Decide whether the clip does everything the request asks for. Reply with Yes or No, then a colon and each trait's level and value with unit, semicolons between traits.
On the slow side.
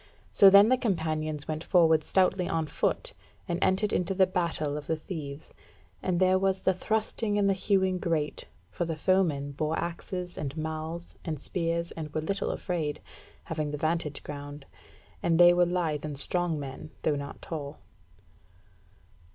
No: average, 165 wpm